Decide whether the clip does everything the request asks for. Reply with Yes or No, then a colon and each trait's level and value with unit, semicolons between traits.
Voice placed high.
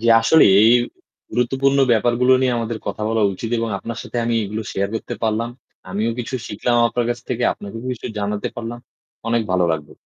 No: low, 115 Hz